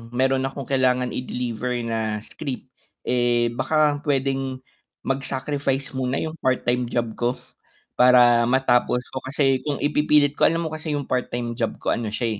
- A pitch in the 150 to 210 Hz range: No, low, 130 Hz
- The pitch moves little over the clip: Yes, narrow, 2.3 semitones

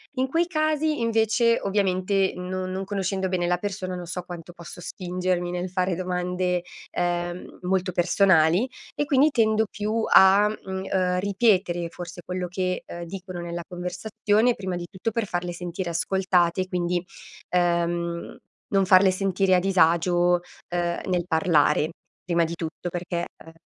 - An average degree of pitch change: No, narrow, 1.9 semitones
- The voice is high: No, medium, 180 Hz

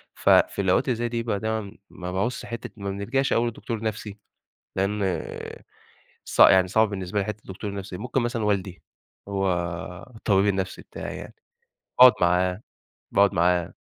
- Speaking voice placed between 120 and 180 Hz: No, low, 100 Hz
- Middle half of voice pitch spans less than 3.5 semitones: Yes, average, 2.7 semitones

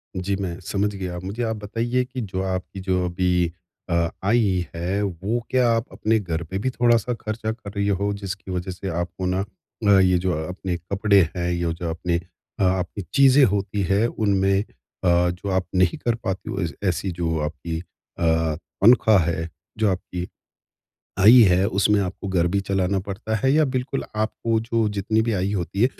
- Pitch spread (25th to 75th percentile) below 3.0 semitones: No, average, 3.3 semitones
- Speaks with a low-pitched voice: Yes, very low, 95 Hz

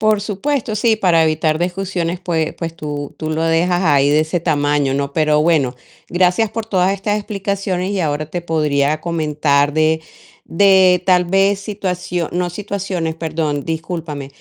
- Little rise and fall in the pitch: No, average, 3.7 semitones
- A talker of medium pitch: Yes, medium, 170 Hz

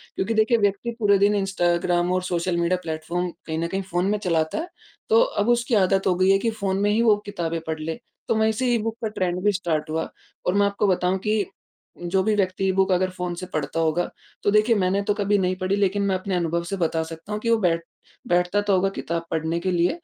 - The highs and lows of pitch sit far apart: No, average, 3.1 semitones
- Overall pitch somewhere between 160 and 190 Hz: Yes, medium, 185 Hz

